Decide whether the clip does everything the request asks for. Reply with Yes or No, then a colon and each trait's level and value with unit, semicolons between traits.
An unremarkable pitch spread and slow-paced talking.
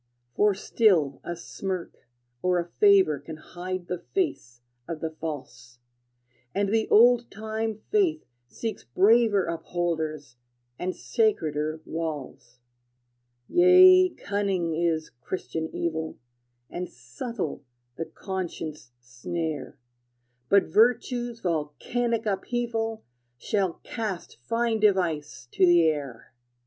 No: wide, 5.9 semitones; slow, 105 wpm